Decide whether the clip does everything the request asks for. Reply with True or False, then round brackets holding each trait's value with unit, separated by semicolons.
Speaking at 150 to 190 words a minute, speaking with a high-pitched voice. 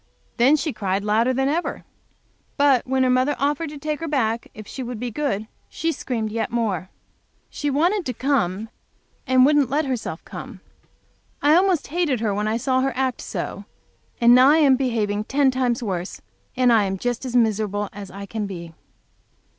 True (185 wpm; 250 Hz)